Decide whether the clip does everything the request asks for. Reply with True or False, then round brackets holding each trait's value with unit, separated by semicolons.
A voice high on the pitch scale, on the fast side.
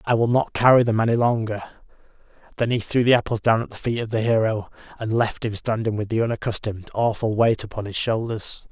False (110 Hz; 215 wpm)